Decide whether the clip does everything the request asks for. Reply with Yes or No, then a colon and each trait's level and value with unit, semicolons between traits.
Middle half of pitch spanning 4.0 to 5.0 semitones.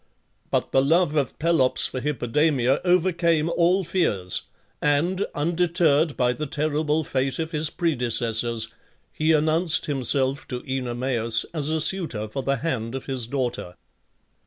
Yes: average, 4.4 semitones